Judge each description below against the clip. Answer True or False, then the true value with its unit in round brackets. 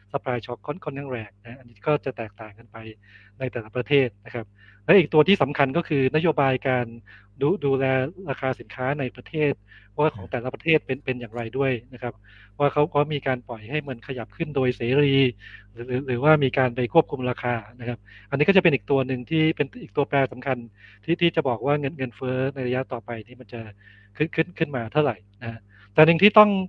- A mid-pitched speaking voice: False (130 Hz)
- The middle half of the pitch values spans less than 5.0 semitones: True (3.5 semitones)